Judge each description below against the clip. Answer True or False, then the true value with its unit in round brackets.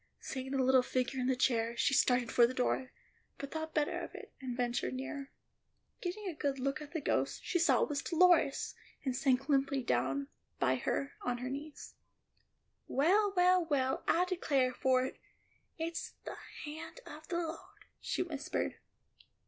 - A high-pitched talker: True (275 Hz)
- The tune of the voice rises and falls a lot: False (3.8 semitones)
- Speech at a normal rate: True (175 wpm)